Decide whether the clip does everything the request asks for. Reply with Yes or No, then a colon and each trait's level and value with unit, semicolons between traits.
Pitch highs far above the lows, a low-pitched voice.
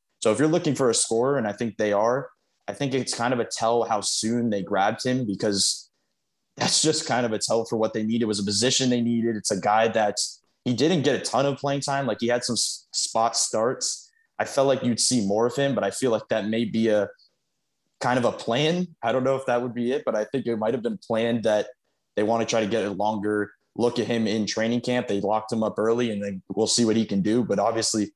No: average, 2.7 semitones; low, 115 Hz